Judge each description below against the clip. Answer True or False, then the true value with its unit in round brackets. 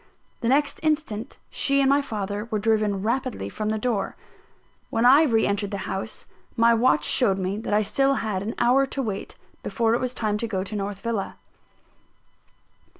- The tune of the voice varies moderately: True (3.8 semitones)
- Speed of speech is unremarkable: True (185 wpm)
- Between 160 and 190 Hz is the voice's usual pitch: False (225 Hz)